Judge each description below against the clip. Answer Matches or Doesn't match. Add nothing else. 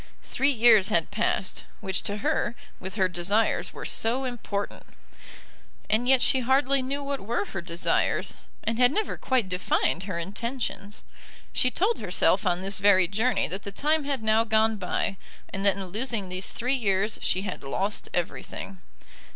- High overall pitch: Matches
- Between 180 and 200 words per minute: Doesn't match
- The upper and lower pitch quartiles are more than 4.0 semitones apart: Matches